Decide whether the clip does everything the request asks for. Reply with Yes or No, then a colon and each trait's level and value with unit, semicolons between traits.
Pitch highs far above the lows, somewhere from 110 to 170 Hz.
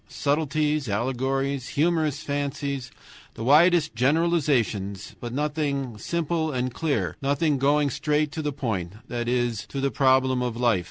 No: average, 3.5 semitones; medium, 140 Hz